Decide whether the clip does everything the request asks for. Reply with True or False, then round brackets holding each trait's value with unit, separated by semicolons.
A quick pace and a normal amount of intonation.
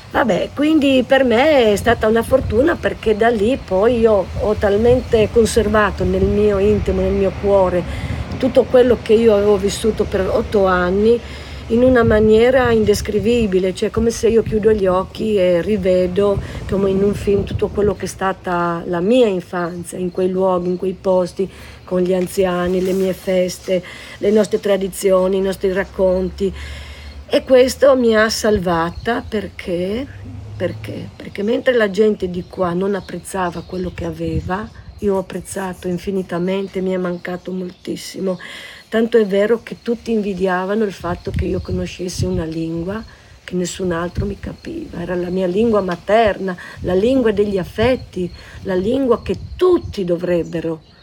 False (155 wpm; 3.2 semitones)